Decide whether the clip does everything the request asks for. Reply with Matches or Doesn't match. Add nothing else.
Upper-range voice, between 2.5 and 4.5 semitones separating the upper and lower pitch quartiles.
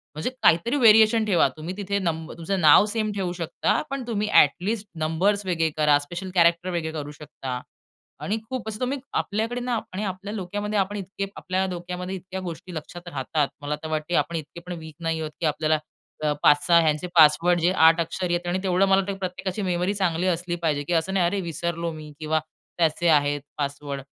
Doesn't match